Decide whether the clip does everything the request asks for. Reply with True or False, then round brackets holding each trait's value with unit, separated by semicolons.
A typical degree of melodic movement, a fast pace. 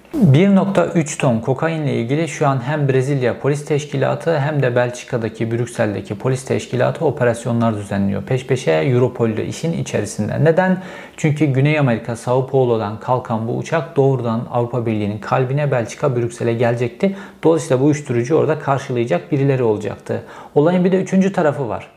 True (4.6 semitones; 145 wpm)